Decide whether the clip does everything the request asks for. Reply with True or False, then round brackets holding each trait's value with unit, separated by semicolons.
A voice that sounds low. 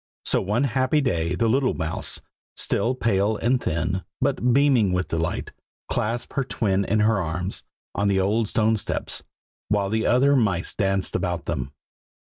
True (105 Hz)